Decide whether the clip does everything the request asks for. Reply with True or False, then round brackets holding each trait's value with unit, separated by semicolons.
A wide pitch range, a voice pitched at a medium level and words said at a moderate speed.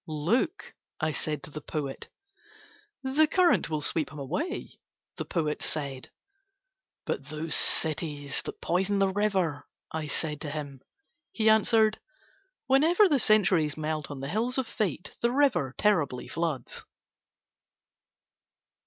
False (6.6 semitones; 165 Hz; 130 wpm)